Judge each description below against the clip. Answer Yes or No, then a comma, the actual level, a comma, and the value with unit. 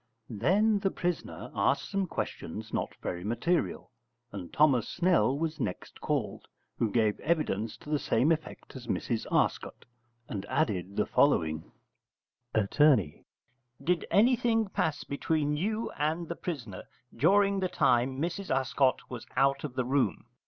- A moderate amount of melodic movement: No, wide, 7.2 semitones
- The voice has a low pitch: No, medium, 145 Hz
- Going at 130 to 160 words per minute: Yes, average, 140 wpm